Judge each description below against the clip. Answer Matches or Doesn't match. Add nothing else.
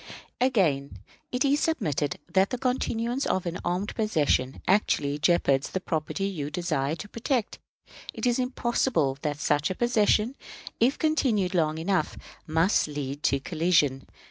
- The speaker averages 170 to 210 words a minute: Doesn't match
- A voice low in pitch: Doesn't match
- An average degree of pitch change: Doesn't match